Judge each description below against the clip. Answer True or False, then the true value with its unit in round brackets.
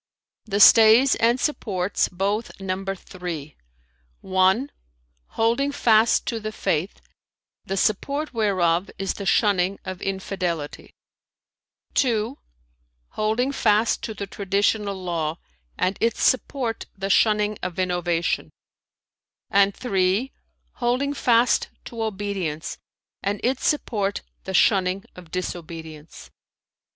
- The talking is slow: True (110 wpm)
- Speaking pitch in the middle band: False (200 Hz)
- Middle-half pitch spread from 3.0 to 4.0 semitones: True (3.6 semitones)